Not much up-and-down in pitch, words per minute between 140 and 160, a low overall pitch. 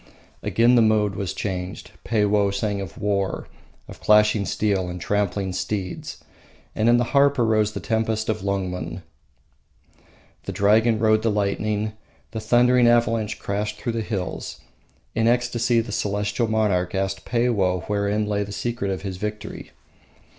Yes: narrow, 2.2 semitones; average, 145 wpm; low, 105 Hz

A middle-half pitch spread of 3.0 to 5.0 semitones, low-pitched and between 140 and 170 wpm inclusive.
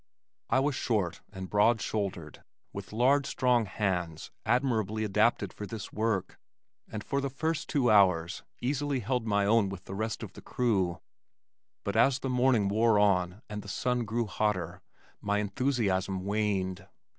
Yes: average, 4.0 semitones; low, 105 Hz; average, 155 wpm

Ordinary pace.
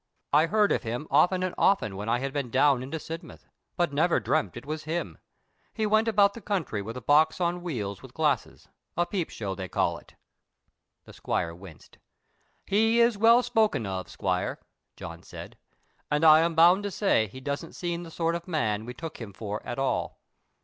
Yes: average, 195 wpm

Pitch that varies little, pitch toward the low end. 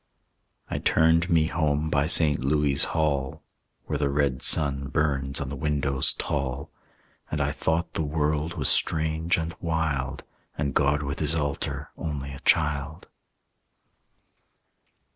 Yes: narrow, 2.2 semitones; very low, 75 Hz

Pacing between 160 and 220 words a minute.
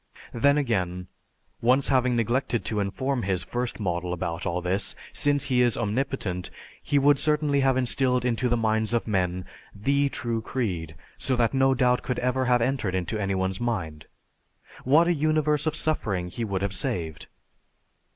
Yes: average, 170 wpm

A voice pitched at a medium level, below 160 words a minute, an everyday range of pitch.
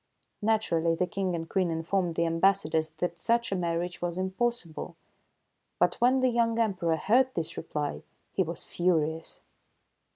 Yes: medium, 175 Hz; average, 150 wpm; average, 3.9 semitones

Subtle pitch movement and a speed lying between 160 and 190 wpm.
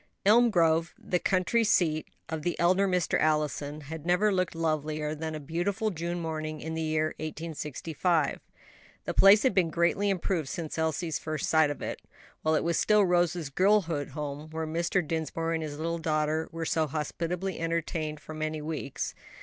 Yes: narrow, 2.2 semitones; average, 175 wpm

